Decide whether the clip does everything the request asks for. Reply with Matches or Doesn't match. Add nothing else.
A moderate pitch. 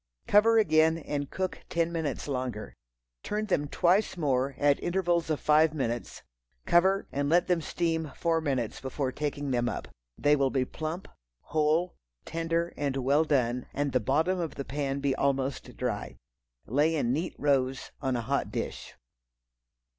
Matches